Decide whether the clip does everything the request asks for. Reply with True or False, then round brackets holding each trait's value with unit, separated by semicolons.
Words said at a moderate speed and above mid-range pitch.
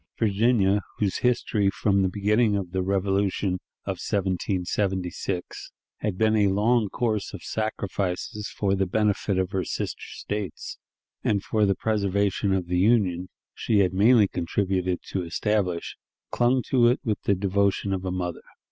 False (150 wpm; 100 Hz)